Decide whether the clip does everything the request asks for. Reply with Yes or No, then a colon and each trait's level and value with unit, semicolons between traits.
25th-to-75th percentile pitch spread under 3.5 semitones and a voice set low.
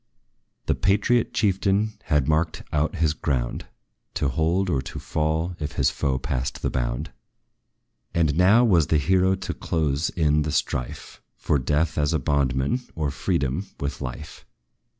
No: average, 4.3 semitones; very low, 75 Hz